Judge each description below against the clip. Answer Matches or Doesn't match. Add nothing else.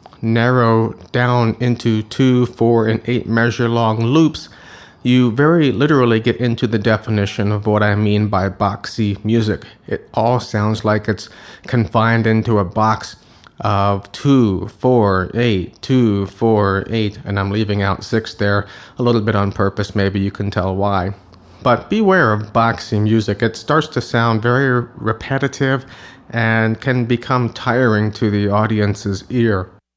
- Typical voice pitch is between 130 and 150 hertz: Doesn't match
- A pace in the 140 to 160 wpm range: Matches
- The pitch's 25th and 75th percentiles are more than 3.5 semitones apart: Doesn't match